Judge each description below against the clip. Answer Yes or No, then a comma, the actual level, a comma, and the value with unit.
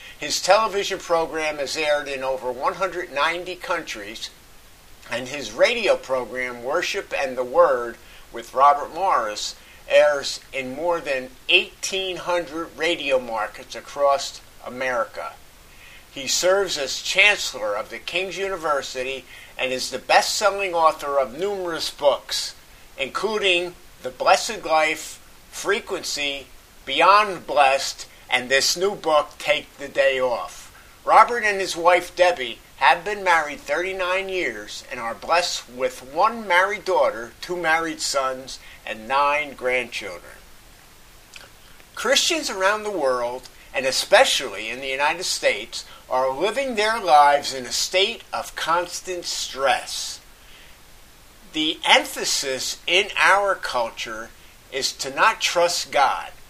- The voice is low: No, medium, 170 Hz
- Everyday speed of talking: No, slow, 120 wpm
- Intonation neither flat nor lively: No, wide, 6.2 semitones